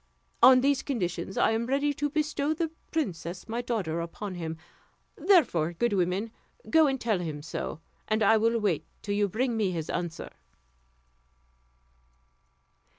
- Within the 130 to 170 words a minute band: Yes, average, 150 wpm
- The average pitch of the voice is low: No, high, 220 Hz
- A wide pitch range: Yes, wide, 7.1 semitones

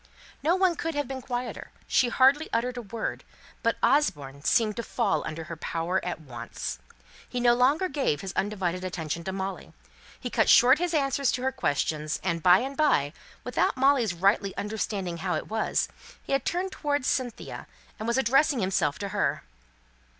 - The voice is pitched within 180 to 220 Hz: No, high, 230 Hz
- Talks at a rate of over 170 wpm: Yes, average, 180 wpm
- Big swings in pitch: Yes, wide, 7.1 semitones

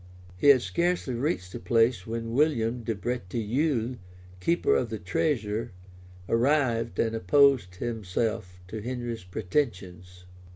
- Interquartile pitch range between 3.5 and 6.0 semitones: Yes, average, 4.6 semitones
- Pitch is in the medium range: No, low, 115 Hz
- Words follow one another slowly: Yes, slow, 120 wpm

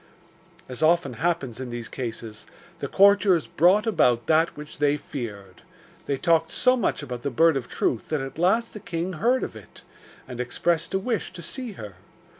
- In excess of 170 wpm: Yes, average, 185 wpm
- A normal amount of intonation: No, wide, 6.7 semitones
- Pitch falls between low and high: Yes, medium, 155 Hz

